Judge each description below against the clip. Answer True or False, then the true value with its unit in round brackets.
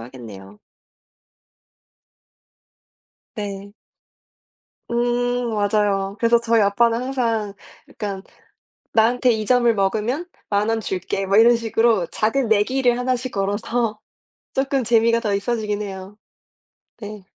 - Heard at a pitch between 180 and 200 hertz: False (220 Hz)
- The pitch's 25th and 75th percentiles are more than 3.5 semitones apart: False (3.0 semitones)